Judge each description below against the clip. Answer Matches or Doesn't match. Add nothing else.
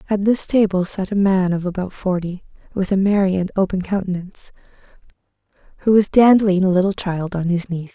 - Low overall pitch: Doesn't match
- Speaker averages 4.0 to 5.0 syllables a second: Doesn't match